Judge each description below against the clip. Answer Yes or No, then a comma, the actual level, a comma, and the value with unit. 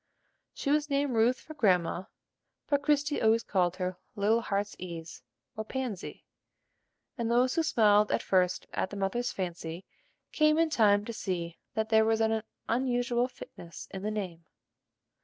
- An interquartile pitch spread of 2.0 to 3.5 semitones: No, average, 4.9 semitones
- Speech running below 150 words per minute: No, average, 160 wpm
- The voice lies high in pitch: Yes, high, 220 Hz